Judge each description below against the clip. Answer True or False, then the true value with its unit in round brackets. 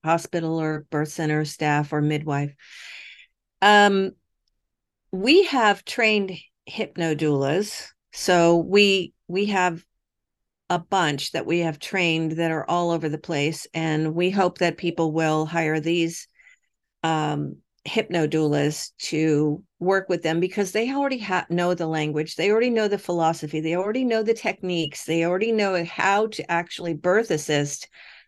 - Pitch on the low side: False (170 Hz)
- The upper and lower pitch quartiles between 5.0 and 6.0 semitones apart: False (3.7 semitones)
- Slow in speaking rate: False (145 wpm)